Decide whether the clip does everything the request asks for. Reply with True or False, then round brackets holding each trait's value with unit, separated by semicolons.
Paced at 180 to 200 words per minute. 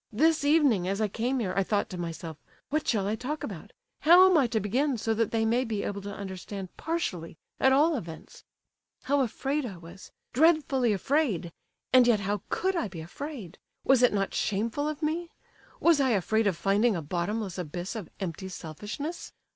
True (185 wpm)